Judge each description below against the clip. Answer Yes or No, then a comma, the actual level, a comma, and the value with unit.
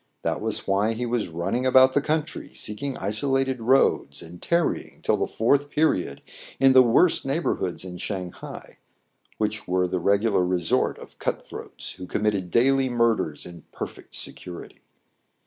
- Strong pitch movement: Yes, wide, 6.5 semitones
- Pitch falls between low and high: No, low, 110 Hz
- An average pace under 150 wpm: No, average, 160 wpm